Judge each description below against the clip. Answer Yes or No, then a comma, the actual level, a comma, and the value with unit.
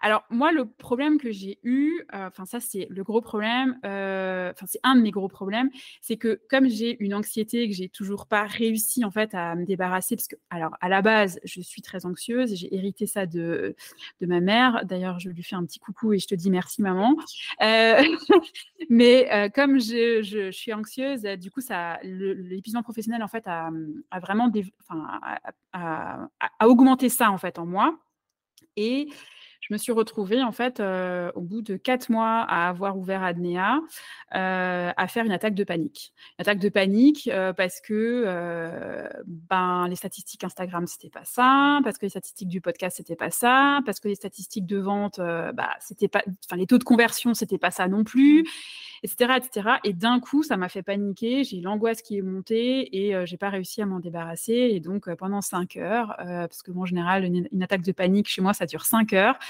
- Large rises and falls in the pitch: No, average, 4.2 semitones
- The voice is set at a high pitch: Yes, high, 205 Hz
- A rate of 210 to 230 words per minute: Yes, average, 215 wpm